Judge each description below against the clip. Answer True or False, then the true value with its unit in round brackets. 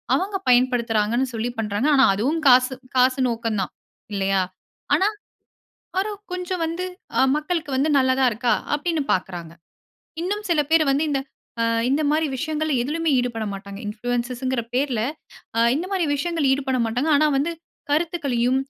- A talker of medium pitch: False (265 Hz)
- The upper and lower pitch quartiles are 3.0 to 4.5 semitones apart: False (4.9 semitones)